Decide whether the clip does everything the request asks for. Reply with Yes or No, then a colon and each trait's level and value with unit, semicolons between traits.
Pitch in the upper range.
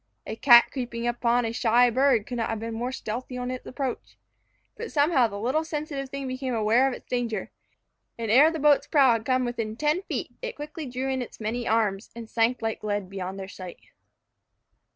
Yes: high, 245 Hz